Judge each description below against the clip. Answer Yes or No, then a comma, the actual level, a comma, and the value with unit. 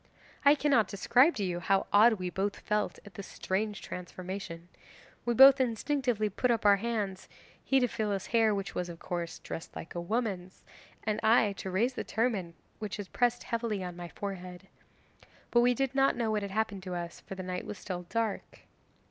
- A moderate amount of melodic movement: Yes, average, 4.0 semitones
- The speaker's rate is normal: Yes, average, 195 wpm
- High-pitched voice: Yes, high, 205 Hz